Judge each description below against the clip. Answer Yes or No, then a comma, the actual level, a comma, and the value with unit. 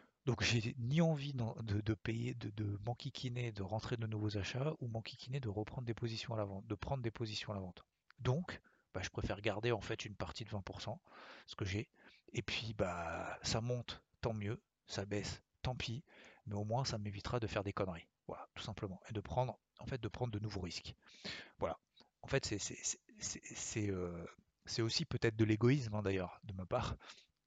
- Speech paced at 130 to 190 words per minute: No, average, 210 wpm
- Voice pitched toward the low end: Yes, low, 115 Hz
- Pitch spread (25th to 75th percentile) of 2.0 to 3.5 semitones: Yes, average, 3.1 semitones